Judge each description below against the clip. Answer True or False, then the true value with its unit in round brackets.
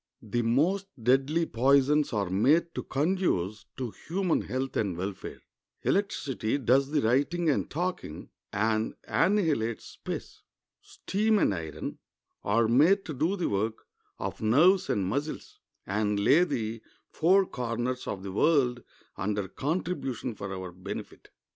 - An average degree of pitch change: False (7.5 semitones)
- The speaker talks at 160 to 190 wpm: False (135 wpm)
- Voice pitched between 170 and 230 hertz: False (130 Hz)